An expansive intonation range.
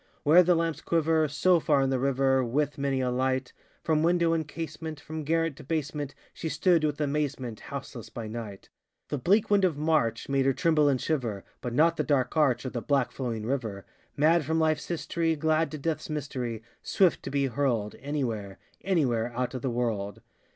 No: average, 4.1 semitones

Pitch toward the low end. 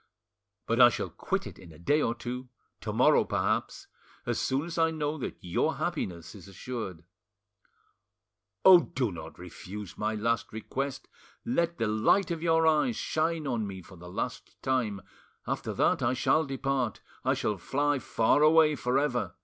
Yes: low, 125 Hz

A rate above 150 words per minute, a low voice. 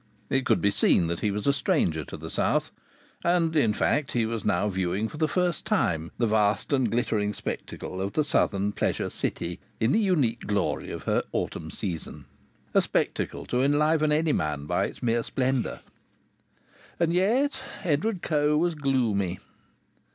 Yes: average, 170 wpm; low, 125 Hz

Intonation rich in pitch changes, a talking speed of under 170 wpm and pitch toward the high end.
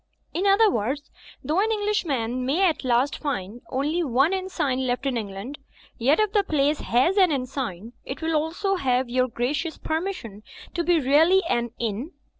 No: wide, 6.0 semitones; average, 185 wpm; very high, 285 Hz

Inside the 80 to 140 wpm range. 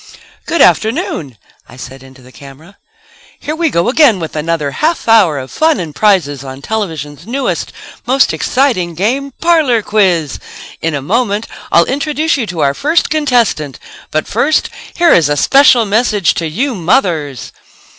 No: average, 155 wpm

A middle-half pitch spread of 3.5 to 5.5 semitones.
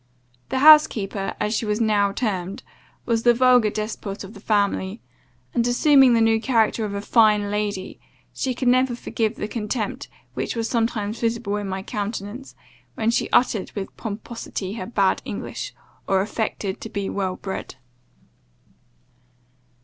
No: average, 2.7 semitones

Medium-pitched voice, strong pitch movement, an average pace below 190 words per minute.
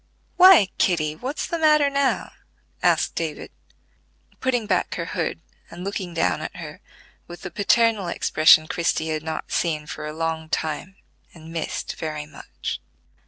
Yes: medium, 170 Hz; wide, 6.1 semitones; average, 150 wpm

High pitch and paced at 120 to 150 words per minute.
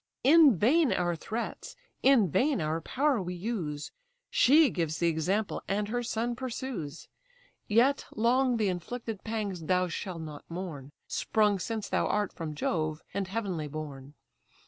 Yes: high, 200 Hz; average, 145 wpm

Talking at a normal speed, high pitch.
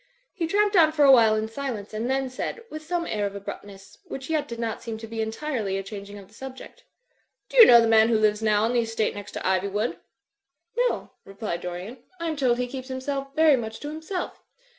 No: fast, 225 wpm; high, 230 Hz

